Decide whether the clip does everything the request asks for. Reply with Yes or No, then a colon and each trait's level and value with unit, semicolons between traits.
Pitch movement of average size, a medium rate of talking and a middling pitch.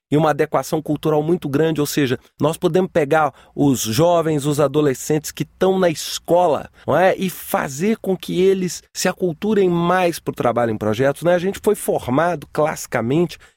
Yes: average, 3.5 semitones; average, 175 wpm; medium, 160 Hz